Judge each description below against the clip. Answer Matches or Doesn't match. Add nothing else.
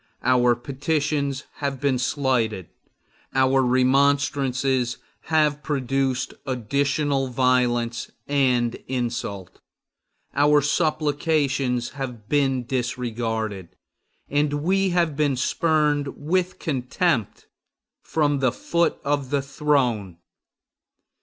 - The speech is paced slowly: Matches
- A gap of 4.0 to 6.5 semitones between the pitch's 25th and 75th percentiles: Doesn't match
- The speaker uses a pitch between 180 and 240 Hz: Doesn't match